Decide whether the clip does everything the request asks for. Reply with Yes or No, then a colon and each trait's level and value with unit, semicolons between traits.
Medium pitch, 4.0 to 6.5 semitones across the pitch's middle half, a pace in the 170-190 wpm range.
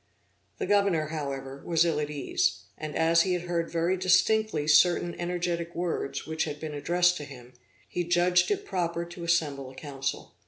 No: medium, 170 Hz; average, 3.0 semitones; average, 180 wpm